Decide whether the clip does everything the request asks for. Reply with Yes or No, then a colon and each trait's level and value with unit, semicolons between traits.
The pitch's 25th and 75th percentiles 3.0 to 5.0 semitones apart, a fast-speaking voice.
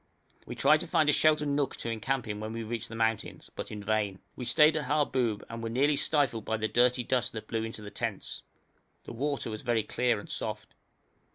Yes: average, 4.3 semitones; fast, 220 wpm